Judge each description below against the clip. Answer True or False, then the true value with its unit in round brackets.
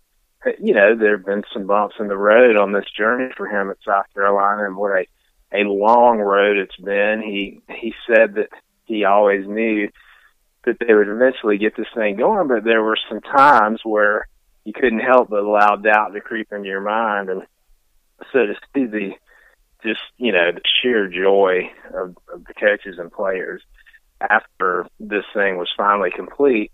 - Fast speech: False (180 wpm)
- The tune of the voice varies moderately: False (1.4 semitones)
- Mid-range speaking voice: False (105 Hz)